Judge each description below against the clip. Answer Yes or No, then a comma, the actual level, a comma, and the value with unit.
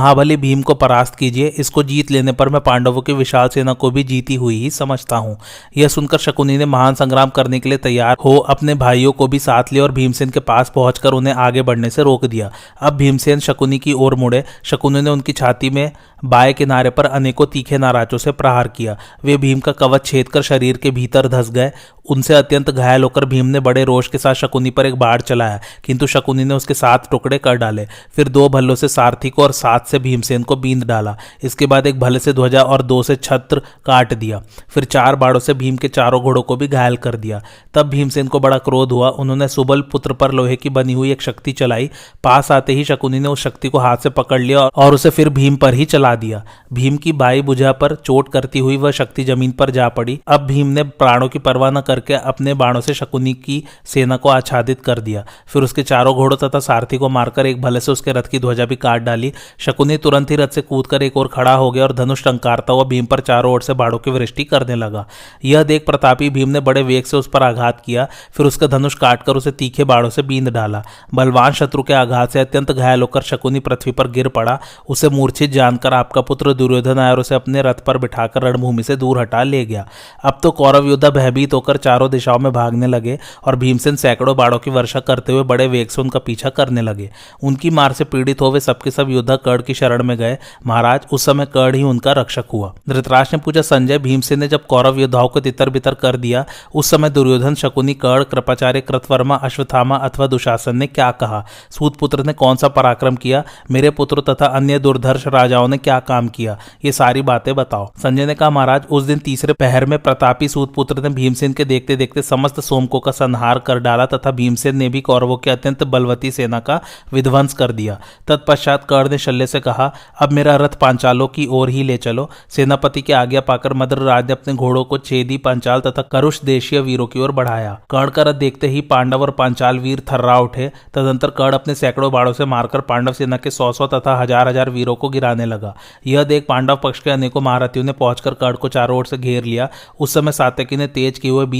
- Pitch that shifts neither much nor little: No, narrow, 1.8 semitones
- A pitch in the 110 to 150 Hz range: Yes, low, 135 Hz